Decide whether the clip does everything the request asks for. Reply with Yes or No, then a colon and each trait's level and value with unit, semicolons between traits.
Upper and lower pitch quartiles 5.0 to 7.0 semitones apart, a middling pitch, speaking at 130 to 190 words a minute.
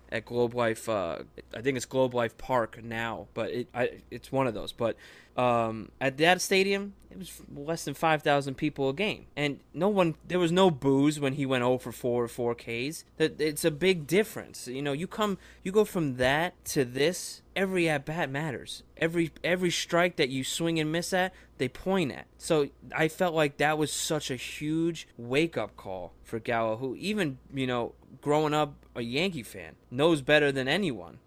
No: average, 5.3 semitones; medium, 145 Hz; average, 200 wpm